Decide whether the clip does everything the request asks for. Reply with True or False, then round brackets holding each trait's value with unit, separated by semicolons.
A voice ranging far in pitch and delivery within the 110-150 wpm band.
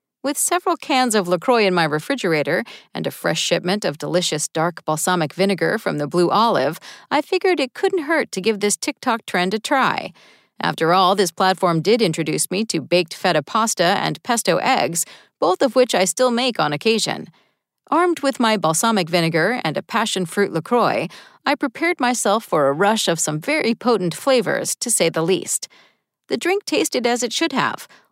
False (6.6 semitones; 185 wpm)